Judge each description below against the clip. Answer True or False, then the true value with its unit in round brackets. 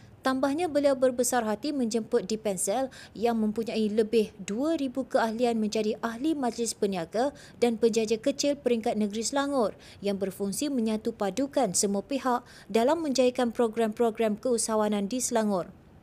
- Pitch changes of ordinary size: True (3.2 semitones)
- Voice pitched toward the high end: True (235 Hz)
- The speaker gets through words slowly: False (125 wpm)